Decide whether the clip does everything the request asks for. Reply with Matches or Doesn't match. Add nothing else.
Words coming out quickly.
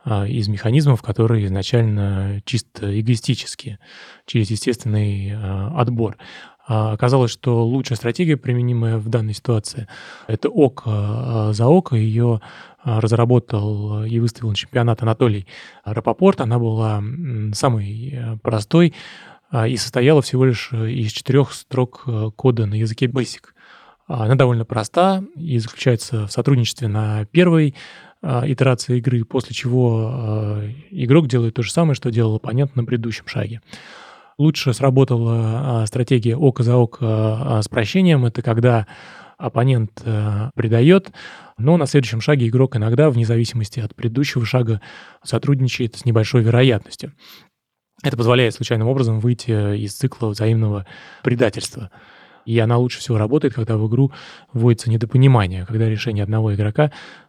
Doesn't match